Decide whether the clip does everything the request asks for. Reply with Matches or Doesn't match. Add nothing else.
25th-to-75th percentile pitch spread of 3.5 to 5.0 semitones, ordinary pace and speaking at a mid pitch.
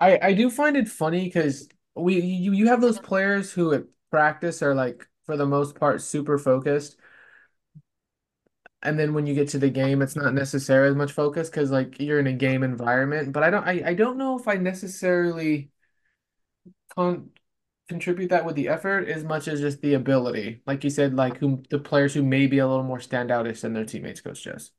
Doesn't match